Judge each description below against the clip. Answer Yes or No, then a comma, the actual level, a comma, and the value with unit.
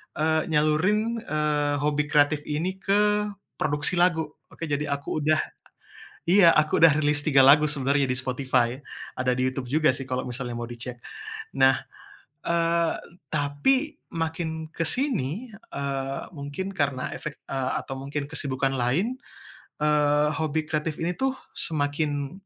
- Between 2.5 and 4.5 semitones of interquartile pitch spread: Yes, average, 3.0 semitones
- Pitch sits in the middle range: Yes, medium, 150 Hz